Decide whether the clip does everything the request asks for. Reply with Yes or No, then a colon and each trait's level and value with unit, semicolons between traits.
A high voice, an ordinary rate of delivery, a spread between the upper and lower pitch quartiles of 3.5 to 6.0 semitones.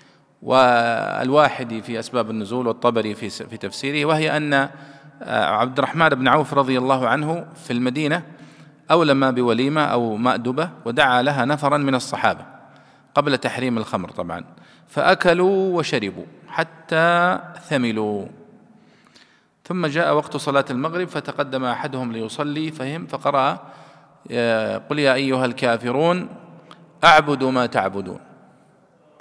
No: low, 135 Hz; average, 110 wpm; average, 4.1 semitones